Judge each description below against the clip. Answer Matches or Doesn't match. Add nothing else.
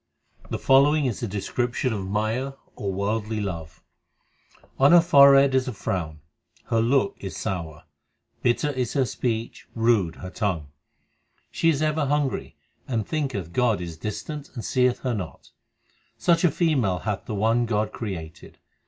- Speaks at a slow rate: Doesn't match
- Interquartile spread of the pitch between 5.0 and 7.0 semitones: Matches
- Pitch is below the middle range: Matches